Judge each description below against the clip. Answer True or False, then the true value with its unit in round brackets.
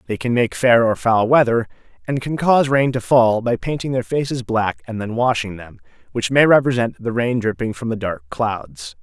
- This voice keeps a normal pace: False (215 wpm)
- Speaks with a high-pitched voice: False (115 Hz)